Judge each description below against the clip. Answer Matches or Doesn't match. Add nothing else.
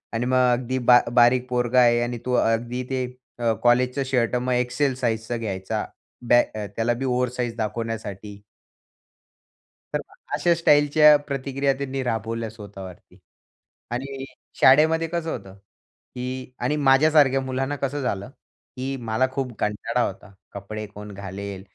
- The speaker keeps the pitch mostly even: Doesn't match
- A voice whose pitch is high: Doesn't match